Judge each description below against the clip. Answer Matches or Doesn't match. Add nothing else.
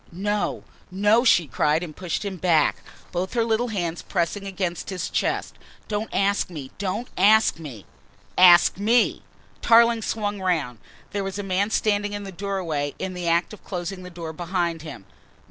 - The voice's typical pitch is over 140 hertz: Matches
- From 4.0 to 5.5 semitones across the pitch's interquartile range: Doesn't match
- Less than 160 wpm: Doesn't match